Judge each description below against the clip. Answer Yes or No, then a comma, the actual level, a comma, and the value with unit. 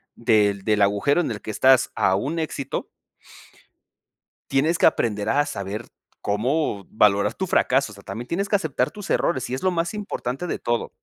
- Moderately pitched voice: No, low, 125 Hz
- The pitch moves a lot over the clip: Yes, wide, 7.4 semitones